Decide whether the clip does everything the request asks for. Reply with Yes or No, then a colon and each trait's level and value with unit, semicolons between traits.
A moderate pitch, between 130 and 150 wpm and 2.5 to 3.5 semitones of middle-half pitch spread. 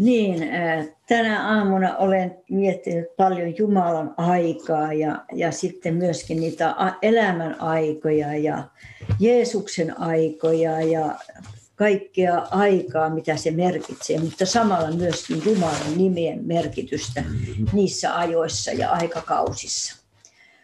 No: medium, 170 Hz; average, 100 wpm; average, 3.1 semitones